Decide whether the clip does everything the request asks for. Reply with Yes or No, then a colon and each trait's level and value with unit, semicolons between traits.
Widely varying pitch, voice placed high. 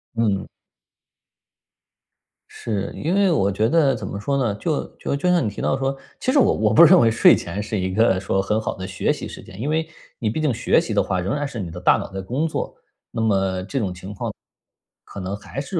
No: wide, 6.4 semitones; low, 110 Hz